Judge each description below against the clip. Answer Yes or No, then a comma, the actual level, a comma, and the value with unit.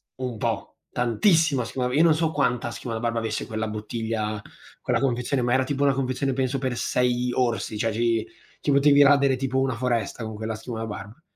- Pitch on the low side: Yes, low, 125 Hz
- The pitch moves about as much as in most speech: Yes, average, 3.1 semitones